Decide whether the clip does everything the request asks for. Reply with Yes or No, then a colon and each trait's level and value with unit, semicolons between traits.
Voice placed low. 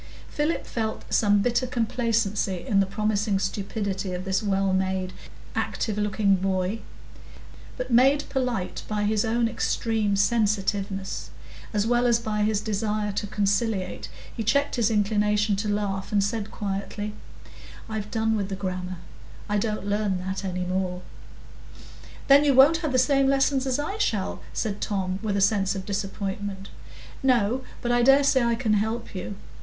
No: high, 210 Hz